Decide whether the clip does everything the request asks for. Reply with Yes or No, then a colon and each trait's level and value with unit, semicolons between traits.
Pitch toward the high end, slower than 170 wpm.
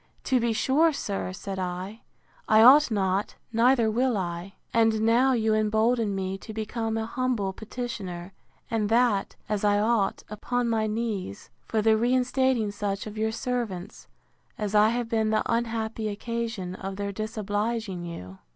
Yes: high, 220 Hz; average, 155 wpm